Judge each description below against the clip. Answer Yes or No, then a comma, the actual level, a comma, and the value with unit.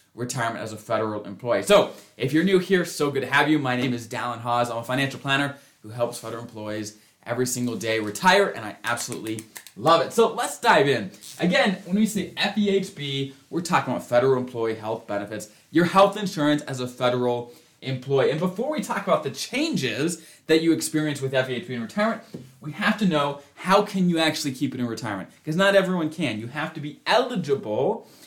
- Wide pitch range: Yes, wide, 6.3 semitones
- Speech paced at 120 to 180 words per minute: No, average, 200 wpm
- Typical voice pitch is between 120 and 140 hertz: Yes, low, 135 Hz